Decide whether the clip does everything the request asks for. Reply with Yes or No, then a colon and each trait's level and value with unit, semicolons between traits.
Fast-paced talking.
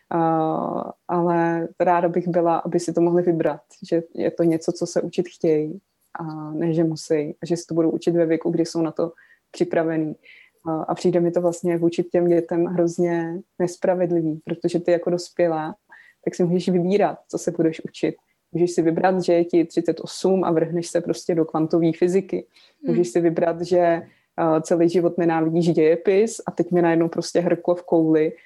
Yes: fast, 190 wpm